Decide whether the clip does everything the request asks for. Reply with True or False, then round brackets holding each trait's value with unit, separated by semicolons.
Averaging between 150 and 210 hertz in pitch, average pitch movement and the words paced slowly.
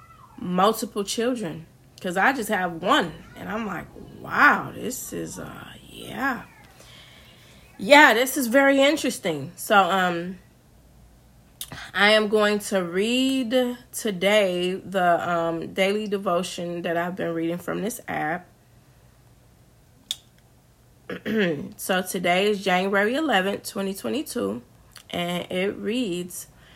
True (190 Hz; 4.1 semitones; 110 wpm)